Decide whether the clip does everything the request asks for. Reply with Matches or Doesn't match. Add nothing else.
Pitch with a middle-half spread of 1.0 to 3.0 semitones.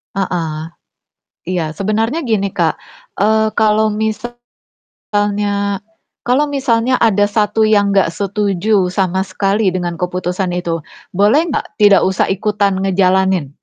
Matches